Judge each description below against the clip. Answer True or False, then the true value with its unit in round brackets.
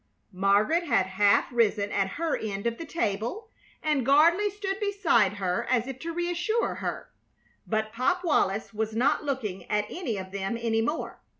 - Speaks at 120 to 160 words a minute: False (170 wpm)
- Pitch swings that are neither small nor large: False (8.5 semitones)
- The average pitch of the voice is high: True (235 Hz)